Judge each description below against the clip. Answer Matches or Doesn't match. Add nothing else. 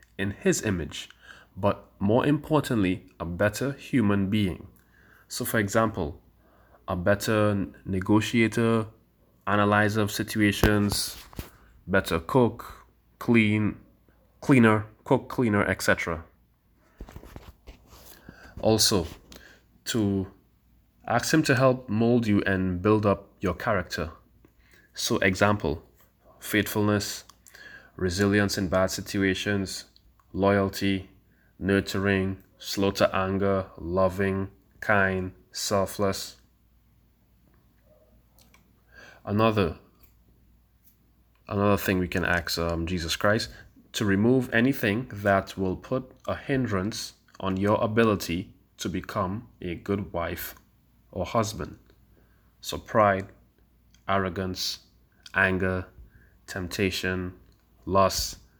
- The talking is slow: Matches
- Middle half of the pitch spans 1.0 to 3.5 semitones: Matches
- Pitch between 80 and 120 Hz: Matches